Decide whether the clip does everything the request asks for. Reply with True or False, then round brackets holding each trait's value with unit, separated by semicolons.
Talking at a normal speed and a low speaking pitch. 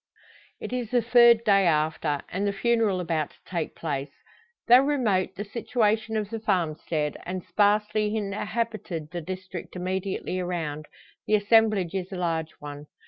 False (155 wpm; 190 Hz)